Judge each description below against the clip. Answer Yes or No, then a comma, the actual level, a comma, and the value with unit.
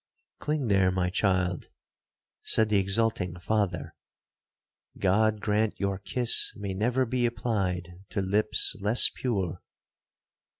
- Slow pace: Yes, slow, 110 wpm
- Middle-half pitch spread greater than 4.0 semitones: No, average, 3.0 semitones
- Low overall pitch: Yes, low, 100 Hz